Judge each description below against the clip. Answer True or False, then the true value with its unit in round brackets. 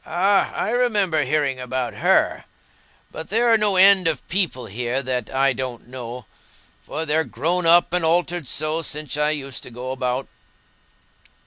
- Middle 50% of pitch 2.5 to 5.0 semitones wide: False (5.5 semitones)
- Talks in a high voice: False (150 Hz)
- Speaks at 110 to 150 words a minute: False (160 wpm)